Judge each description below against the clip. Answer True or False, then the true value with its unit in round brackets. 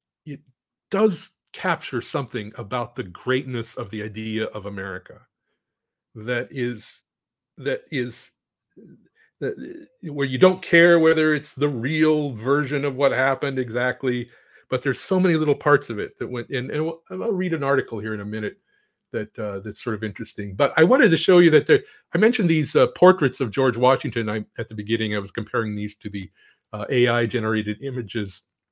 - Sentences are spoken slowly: False (170 wpm)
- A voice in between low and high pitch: False (125 Hz)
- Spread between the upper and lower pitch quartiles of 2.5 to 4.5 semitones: False (5.5 semitones)